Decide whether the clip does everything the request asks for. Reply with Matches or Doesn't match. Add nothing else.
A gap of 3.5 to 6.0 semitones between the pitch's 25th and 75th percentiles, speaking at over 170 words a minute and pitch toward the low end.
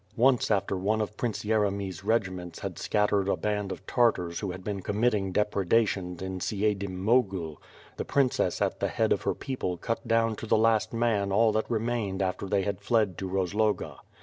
Doesn't match